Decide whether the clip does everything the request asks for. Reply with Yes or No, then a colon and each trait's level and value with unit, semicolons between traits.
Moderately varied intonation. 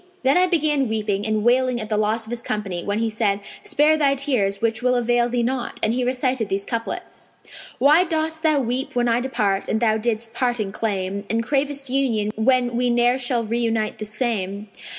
Yes: average, 3.2 semitones